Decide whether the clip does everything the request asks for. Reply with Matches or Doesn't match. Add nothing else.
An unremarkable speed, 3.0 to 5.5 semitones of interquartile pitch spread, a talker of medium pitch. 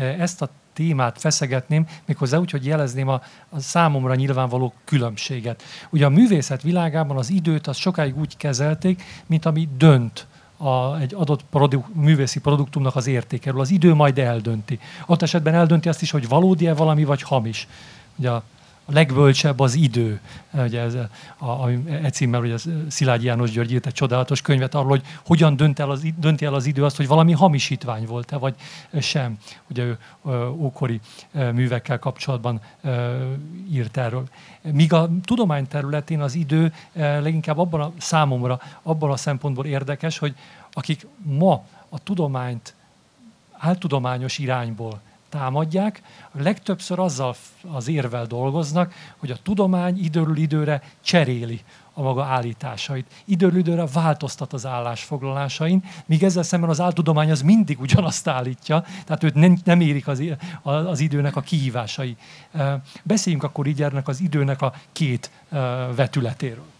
Matches